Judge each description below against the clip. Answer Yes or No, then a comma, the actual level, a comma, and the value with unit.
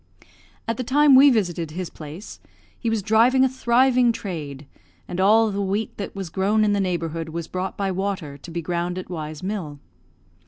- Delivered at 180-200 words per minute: Yes, average, 195 wpm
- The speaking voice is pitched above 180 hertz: Yes, high, 190 Hz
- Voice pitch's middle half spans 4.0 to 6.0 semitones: Yes, average, 4.8 semitones